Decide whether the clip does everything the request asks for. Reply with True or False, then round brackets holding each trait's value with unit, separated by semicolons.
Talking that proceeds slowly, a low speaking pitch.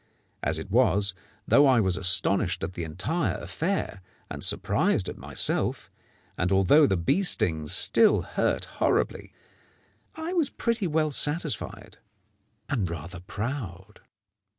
True (130 wpm; 105 Hz)